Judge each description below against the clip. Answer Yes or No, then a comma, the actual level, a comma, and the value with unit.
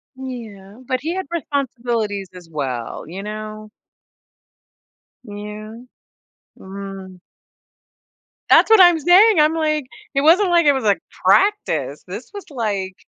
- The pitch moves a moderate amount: No, wide, 7.9 semitones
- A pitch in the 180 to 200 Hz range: No, high, 230 Hz